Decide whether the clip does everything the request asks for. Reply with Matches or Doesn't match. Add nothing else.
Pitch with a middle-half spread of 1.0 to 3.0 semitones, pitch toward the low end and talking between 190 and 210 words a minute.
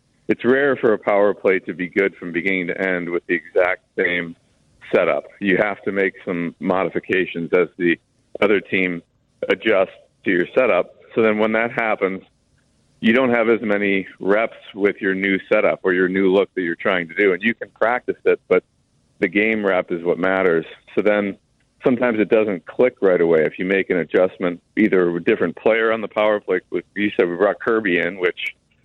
Matches